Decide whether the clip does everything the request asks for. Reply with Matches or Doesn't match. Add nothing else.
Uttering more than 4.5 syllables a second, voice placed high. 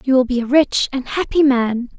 Matches